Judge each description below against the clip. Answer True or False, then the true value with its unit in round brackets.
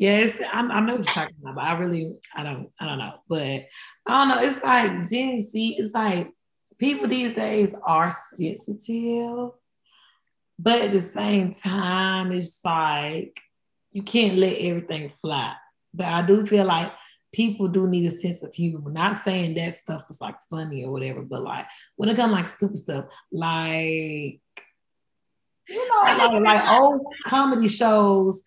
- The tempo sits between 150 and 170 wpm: True (160 wpm)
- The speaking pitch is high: True (195 Hz)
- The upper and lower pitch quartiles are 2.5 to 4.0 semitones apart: False (5.2 semitones)